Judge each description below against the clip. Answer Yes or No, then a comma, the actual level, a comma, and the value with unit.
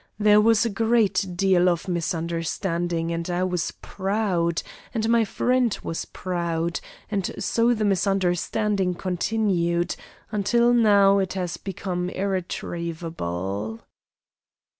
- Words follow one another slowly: Yes, slow, 110 wpm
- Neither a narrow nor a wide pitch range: Yes, average, 3.5 semitones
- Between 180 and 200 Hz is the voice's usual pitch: Yes, medium, 185 Hz